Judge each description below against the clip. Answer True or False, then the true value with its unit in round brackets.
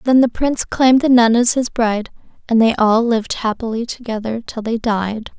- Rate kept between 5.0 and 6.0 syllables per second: True (5.4 syllables/s)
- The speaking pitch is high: True (230 Hz)